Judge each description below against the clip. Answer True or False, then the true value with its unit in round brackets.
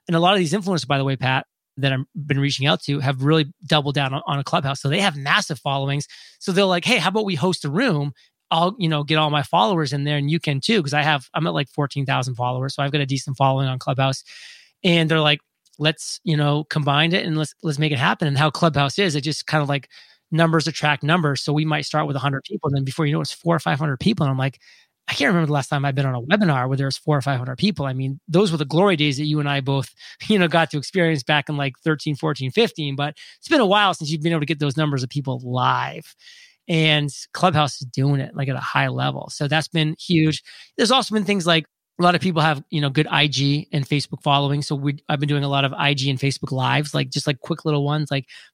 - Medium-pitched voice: True (150 Hz)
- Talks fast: True (275 wpm)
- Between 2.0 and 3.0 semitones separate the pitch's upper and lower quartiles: True (2.7 semitones)